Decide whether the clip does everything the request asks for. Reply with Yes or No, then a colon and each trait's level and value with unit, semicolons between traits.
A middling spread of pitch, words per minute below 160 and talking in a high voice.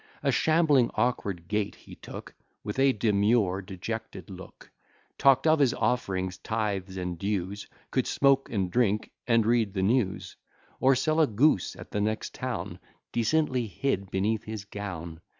No: average, 4.5 semitones; average, 150 wpm; low, 110 Hz